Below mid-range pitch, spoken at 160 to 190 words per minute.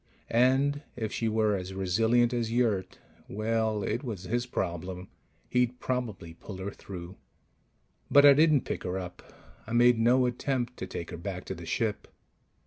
Yes: low, 110 Hz; average, 165 wpm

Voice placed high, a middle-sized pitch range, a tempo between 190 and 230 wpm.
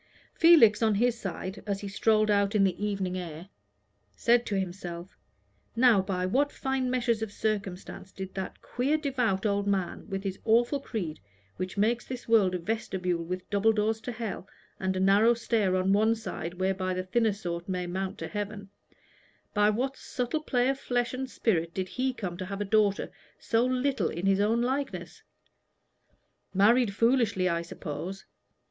No: high, 205 Hz; average, 3.9 semitones; average, 175 wpm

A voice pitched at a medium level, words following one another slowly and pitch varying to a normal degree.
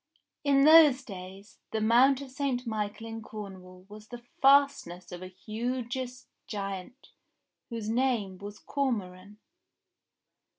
No: high, 225 Hz; slow, 120 wpm; average, 4.8 semitones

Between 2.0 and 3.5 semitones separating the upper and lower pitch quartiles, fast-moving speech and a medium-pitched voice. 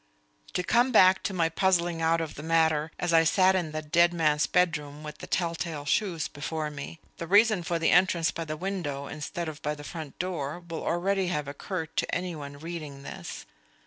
Yes: average, 2.8 semitones; fast, 210 wpm; medium, 165 Hz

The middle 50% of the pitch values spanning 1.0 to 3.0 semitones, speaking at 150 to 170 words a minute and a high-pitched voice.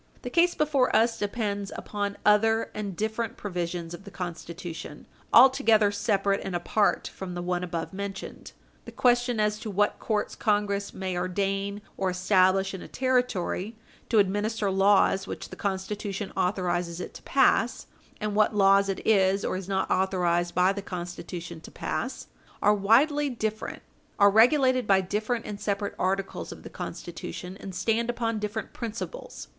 Yes: average, 2.7 semitones; average, 160 wpm; high, 200 Hz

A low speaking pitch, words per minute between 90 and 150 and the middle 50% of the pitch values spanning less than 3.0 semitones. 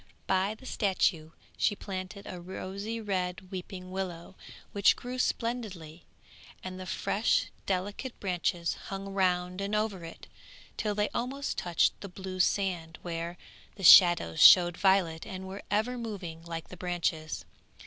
No: high, 190 Hz; average, 140 wpm; narrow, 2.5 semitones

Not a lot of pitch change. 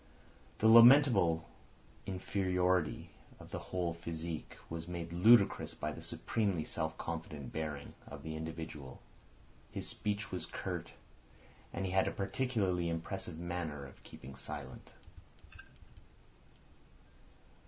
No: average, 3.5 semitones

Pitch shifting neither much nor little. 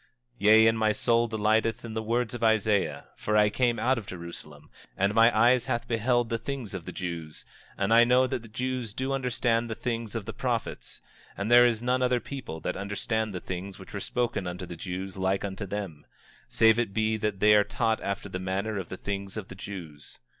Yes: average, 3.3 semitones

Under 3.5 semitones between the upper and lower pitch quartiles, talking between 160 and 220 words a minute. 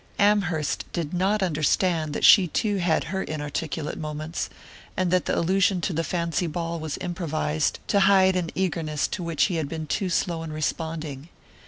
Yes: average, 3.0 semitones; average, 175 wpm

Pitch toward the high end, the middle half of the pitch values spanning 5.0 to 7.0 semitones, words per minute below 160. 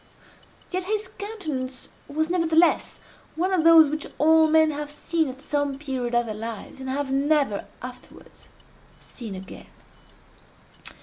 No: very high, 295 Hz; average, 3.7 semitones; slow, 135 wpm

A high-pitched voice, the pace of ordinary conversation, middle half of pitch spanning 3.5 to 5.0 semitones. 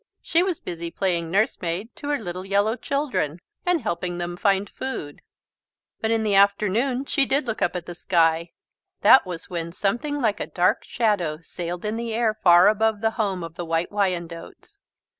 Yes: high, 200 Hz; average, 185 wpm; average, 4.6 semitones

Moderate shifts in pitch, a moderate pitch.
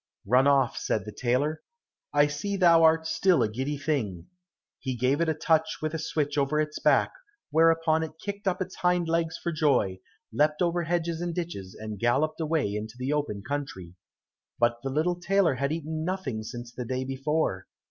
Yes: average, 4.4 semitones; medium, 150 Hz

